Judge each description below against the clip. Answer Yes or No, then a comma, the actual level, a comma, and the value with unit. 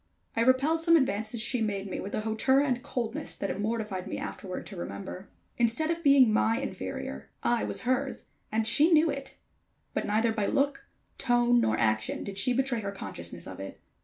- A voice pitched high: Yes, high, 230 Hz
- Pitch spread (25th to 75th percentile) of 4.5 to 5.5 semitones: Yes, average, 5.0 semitones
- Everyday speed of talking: Yes, average, 190 wpm